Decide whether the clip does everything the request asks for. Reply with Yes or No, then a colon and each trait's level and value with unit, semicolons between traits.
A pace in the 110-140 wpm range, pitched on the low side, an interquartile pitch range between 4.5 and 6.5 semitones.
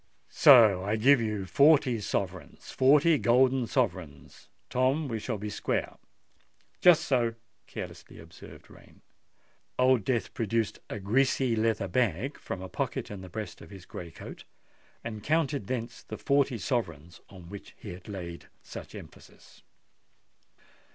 Yes: slow, 135 wpm; low, 115 Hz; average, 5.0 semitones